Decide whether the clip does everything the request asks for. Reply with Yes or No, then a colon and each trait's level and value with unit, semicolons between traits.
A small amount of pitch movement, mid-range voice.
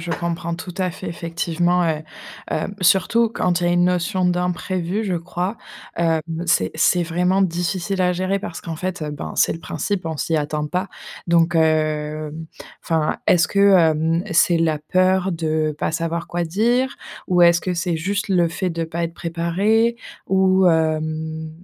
Yes: narrow, 2.3 semitones; medium, 170 Hz